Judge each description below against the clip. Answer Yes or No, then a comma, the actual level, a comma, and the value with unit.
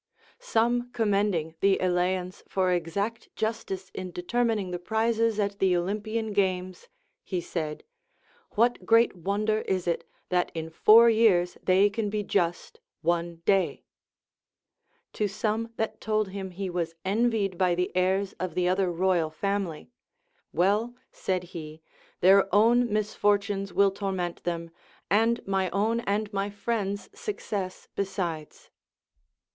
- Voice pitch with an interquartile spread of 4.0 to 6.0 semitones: No, average, 3.1 semitones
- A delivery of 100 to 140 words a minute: Yes, slow, 135 wpm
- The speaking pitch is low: No, high, 195 Hz